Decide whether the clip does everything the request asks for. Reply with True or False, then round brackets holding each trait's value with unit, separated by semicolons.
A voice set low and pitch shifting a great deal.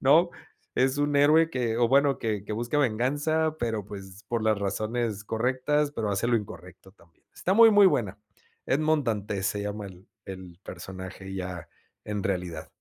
True (110 Hz; 6.4 semitones)